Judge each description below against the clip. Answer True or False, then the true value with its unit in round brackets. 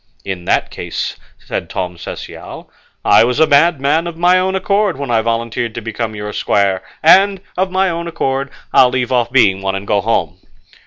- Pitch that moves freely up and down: True (8.4 semitones)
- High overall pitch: False (125 Hz)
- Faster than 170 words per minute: True (190 wpm)